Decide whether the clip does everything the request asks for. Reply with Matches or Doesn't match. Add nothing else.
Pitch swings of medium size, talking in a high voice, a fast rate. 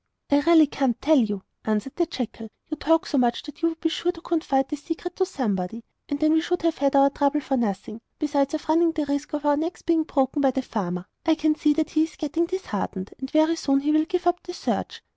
Matches